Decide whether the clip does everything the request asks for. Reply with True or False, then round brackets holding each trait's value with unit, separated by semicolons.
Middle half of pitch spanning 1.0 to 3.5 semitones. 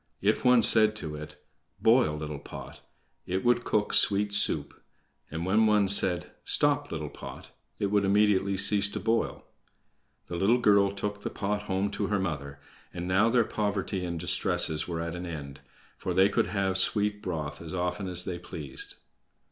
True (3.2 semitones)